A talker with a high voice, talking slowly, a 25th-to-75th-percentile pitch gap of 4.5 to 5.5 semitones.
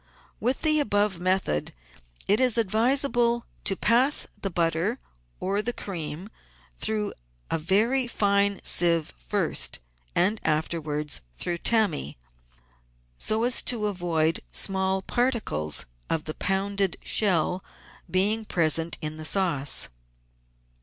Yes: high, 195 Hz; slow, 110 wpm; average, 5.0 semitones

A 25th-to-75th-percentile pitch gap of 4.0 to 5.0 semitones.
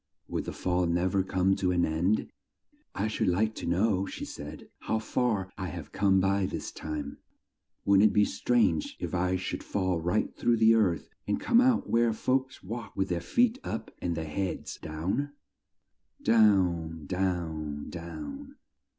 Yes: average, 4.3 semitones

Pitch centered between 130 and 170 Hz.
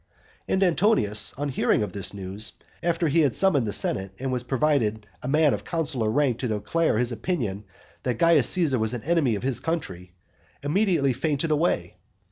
Yes: low, 135 Hz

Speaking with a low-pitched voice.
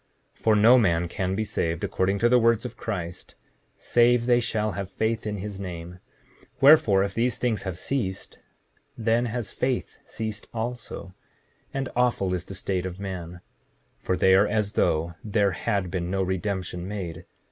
Yes: low, 100 Hz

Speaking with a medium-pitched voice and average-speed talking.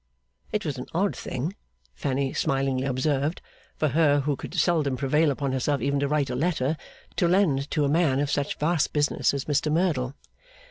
Yes: medium, 145 Hz; average, 185 wpm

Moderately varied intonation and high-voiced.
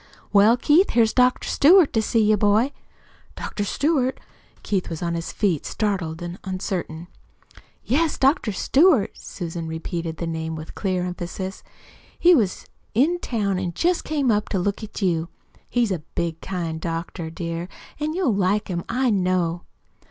No: wide, 6.2 semitones; high, 195 Hz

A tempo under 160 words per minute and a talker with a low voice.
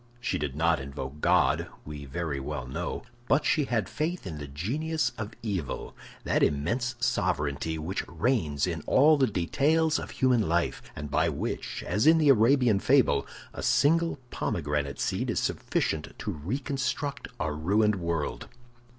Yes: average, 150 wpm; very low, 95 Hz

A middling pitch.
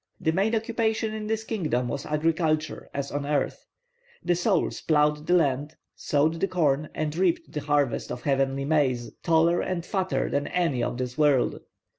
Yes: medium, 155 Hz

